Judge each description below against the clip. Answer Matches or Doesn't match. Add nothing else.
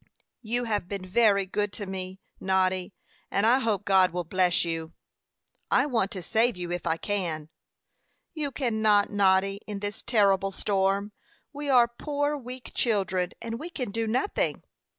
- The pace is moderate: Matches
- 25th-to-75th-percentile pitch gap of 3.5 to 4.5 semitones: Matches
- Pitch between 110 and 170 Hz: Doesn't match